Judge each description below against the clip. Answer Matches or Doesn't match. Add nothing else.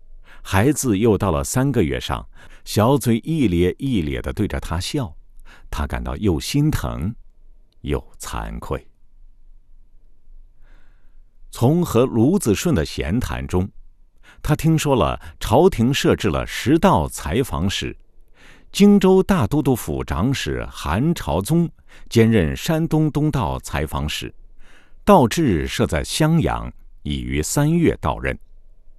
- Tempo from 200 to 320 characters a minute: Doesn't match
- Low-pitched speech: Matches